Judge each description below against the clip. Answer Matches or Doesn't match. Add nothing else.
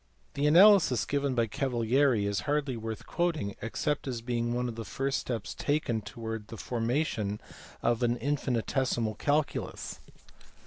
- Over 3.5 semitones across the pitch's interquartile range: Matches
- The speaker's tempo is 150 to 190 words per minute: Doesn't match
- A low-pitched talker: Matches